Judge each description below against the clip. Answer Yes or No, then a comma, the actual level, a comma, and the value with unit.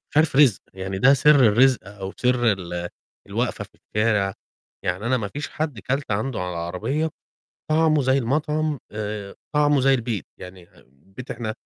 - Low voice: Yes, low, 120 Hz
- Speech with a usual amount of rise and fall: No, wide, 6.2 semitones